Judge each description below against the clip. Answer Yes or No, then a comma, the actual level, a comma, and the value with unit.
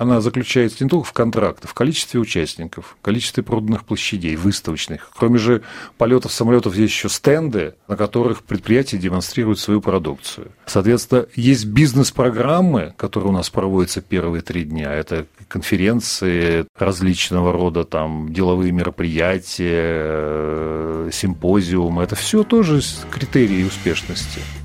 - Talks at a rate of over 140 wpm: No, average, 120 wpm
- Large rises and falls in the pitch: Yes, wide, 5.7 semitones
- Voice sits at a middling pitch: No, low, 100 Hz